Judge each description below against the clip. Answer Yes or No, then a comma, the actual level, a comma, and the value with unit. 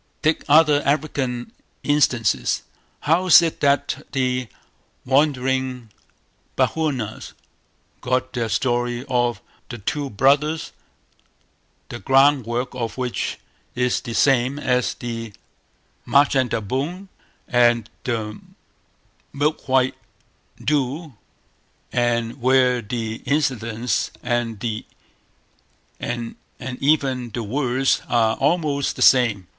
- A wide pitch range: No, average, 2.9 semitones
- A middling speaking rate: No, slow, 95 wpm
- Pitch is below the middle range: Yes, low, 125 Hz